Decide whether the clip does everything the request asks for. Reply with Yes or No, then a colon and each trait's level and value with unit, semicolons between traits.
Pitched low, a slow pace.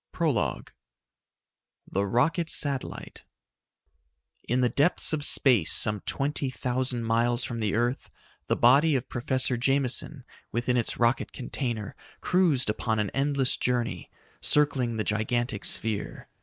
Yes: low, 125 Hz; slow, 130 wpm